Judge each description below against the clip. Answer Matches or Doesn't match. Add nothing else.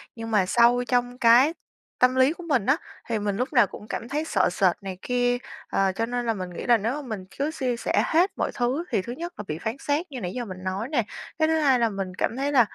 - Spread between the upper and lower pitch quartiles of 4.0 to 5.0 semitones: Matches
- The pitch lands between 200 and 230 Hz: Doesn't match